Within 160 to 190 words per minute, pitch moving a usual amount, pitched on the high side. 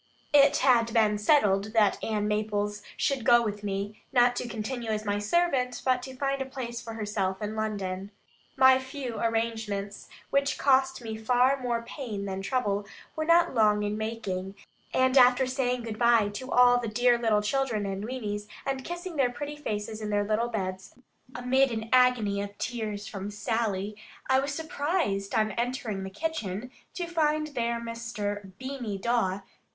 Yes: average, 170 wpm; average, 3.8 semitones; high, 230 Hz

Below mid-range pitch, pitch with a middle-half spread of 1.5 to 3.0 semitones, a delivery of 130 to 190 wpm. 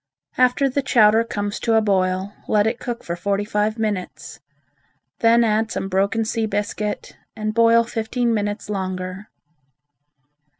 No: high, 215 Hz; narrow, 2.4 semitones; average, 140 wpm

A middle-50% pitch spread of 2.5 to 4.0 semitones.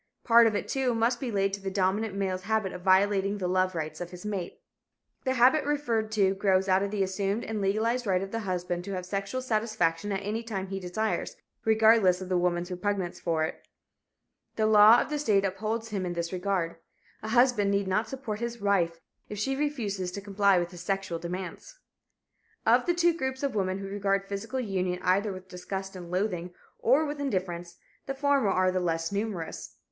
Yes: average, 3.2 semitones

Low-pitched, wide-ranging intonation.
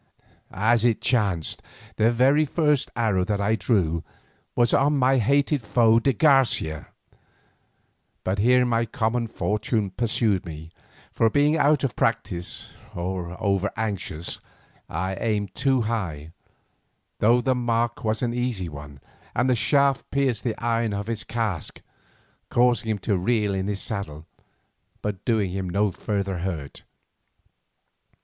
No: low, 110 Hz; average, 4.2 semitones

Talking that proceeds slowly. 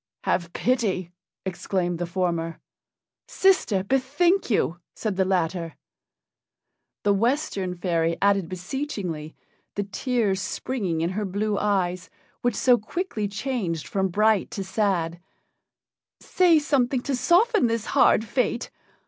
Yes: slow, 120 wpm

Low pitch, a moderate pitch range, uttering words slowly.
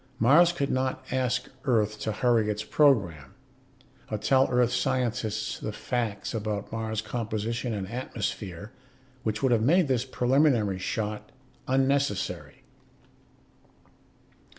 Yes: low, 115 Hz; average, 3.5 semitones; slow, 115 wpm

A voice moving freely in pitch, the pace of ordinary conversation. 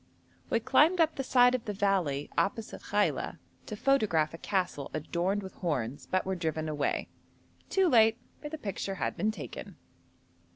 Yes: wide, 6.6 semitones; average, 165 wpm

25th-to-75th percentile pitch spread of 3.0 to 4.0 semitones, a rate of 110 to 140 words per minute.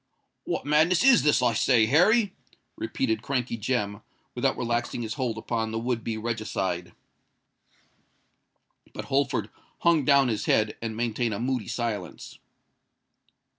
Yes: average, 3.7 semitones; slow, 135 wpm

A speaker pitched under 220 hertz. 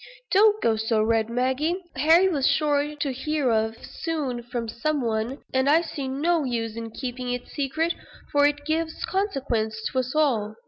No: very high, 270 Hz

